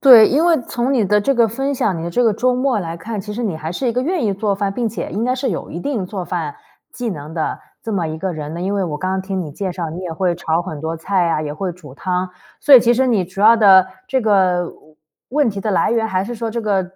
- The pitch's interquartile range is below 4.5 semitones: No, average, 4.9 semitones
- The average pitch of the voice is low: No, high, 195 Hz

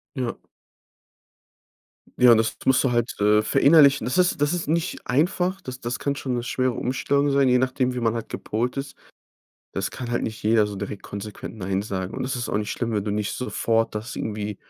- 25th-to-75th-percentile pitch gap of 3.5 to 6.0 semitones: Yes, average, 4.1 semitones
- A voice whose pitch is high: No, low, 120 Hz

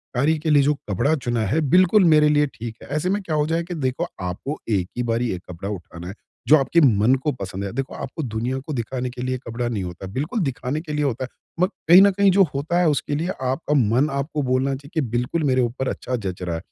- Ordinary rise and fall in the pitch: Yes, average, 4.7 semitones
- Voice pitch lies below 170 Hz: Yes, low, 135 Hz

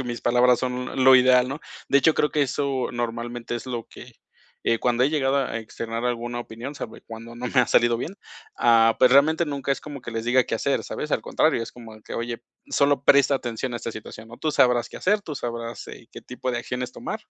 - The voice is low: Yes, low, 125 Hz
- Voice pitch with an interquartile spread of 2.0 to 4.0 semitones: Yes, narrow, 2.6 semitones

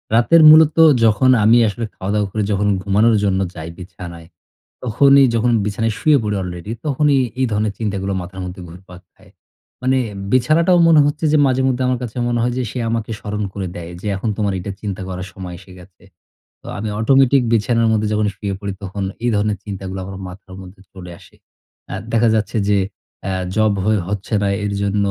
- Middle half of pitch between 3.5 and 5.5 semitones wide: Yes, average, 3.8 semitones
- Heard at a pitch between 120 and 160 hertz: No, low, 105 Hz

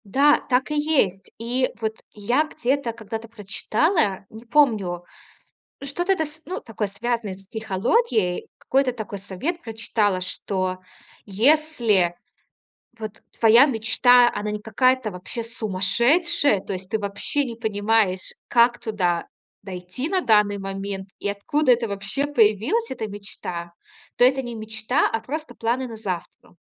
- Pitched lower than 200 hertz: No, high, 225 Hz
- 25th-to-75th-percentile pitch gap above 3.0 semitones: Yes, average, 4.6 semitones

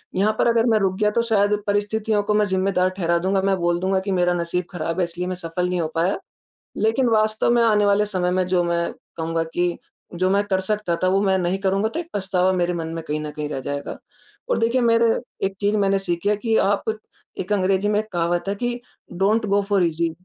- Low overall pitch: No, high, 190 Hz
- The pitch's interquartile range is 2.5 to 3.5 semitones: Yes, average, 3.1 semitones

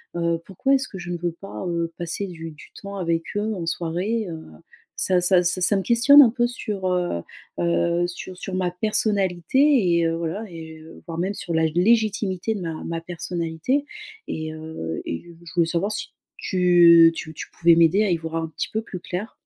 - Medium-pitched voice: Yes, medium, 175 Hz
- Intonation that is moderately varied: Yes, average, 3.3 semitones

